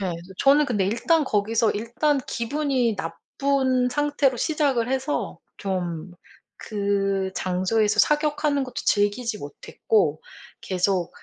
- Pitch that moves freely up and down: Yes, wide, 6.0 semitones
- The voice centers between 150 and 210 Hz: No, high, 225 Hz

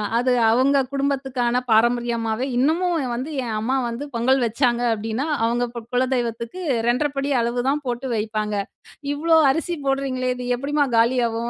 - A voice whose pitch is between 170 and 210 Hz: No, high, 245 Hz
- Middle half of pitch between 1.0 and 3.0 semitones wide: Yes, average, 2.7 semitones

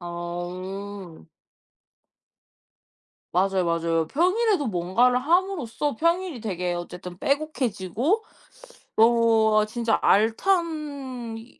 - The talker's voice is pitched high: Yes, high, 225 Hz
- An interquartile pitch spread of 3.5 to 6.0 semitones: No, wide, 8.1 semitones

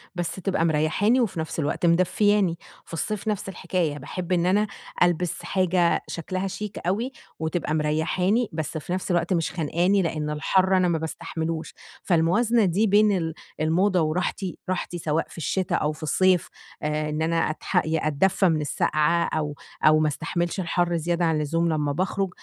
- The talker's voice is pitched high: No, medium, 170 Hz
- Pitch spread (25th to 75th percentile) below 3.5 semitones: Yes, average, 3.0 semitones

